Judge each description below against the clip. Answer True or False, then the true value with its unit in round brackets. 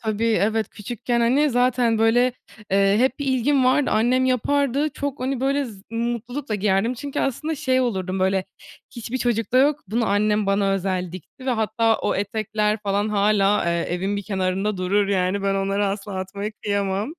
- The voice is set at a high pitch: True (215 Hz)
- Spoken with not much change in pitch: False (4.1 semitones)